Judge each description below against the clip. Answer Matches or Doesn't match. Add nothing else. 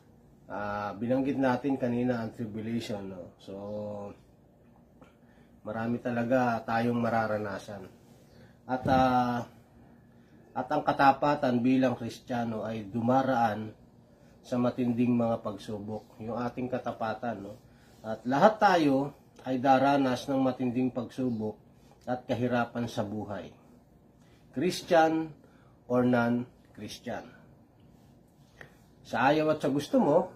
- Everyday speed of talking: Doesn't match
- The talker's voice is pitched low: Matches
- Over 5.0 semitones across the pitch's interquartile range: Doesn't match